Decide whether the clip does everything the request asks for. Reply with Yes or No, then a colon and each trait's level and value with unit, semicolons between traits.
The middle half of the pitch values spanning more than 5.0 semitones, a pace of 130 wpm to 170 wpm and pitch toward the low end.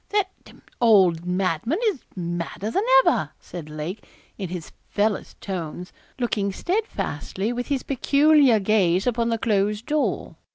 No: wide, 5.5 semitones; average, 140 wpm; high, 210 Hz